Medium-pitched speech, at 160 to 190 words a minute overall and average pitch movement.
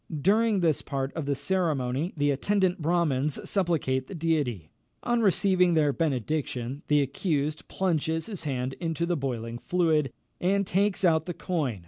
No: medium, 160 Hz; average, 150 wpm; average, 4.8 semitones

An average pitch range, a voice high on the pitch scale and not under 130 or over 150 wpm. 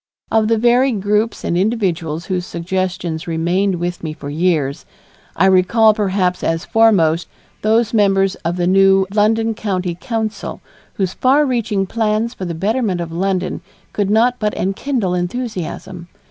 Yes: average, 3.8 semitones; high, 195 Hz; average, 145 wpm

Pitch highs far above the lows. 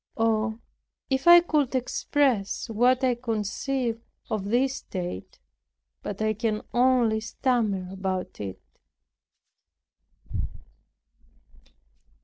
No: average, 3.7 semitones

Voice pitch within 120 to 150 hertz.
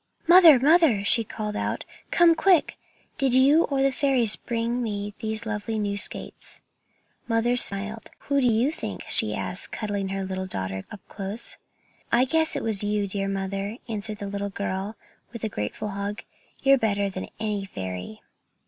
No: high, 215 Hz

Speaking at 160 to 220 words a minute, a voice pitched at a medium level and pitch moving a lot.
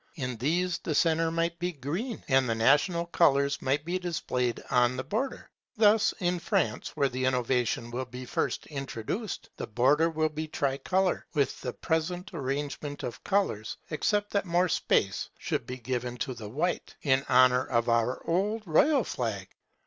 Yes: average, 165 wpm; medium, 145 Hz; wide, 5.7 semitones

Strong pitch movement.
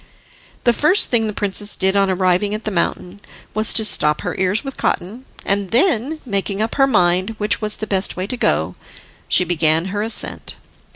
No: average, 3.3 semitones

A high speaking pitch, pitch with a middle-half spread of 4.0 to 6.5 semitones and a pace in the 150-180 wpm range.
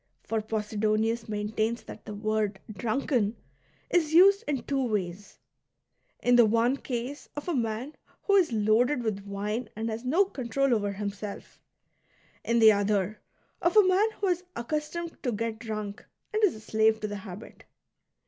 Yes: high, 225 Hz; average, 4.6 semitones; average, 165 wpm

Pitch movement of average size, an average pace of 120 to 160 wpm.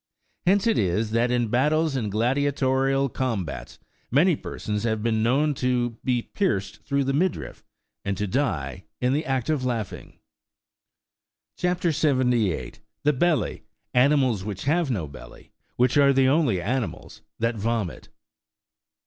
Yes: average, 4.5 semitones; average, 140 wpm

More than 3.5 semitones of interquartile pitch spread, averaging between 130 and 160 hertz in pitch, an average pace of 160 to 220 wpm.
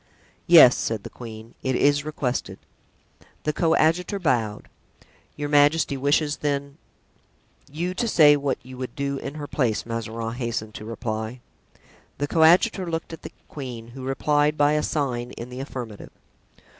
No: average, 4.1 semitones; medium, 140 Hz; average, 150 wpm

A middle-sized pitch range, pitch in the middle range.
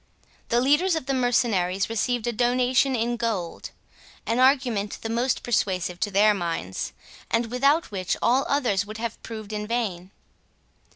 No: average, 3.6 semitones; high, 230 Hz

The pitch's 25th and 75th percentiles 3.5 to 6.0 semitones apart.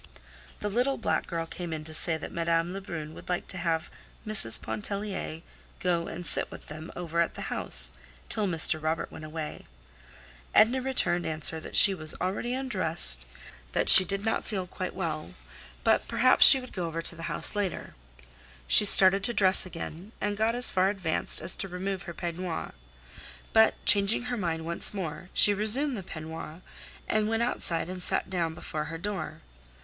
Yes: average, 4.1 semitones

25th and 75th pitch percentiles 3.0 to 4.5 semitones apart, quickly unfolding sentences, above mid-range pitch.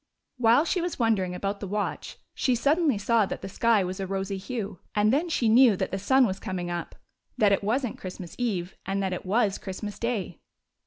Yes: average, 3.9 semitones; fast, 215 wpm; high, 205 Hz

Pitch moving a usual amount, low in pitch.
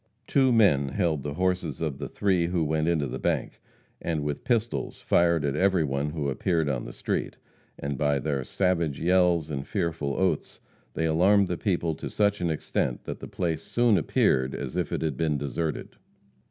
Yes: average, 4.0 semitones; very low, 80 Hz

